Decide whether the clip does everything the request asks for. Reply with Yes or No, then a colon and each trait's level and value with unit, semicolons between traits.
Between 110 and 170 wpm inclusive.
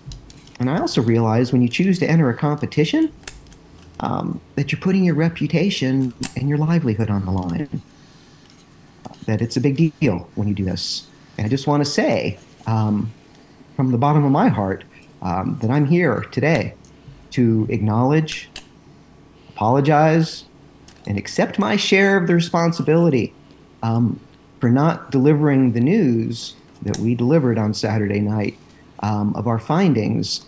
Yes: average, 150 wpm